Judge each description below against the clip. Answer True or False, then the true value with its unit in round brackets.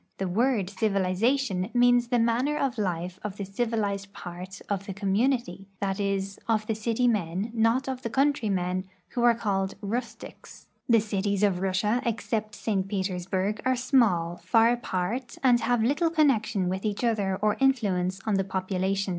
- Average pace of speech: True (170 wpm)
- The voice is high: True (210 Hz)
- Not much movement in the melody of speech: False (3.7 semitones)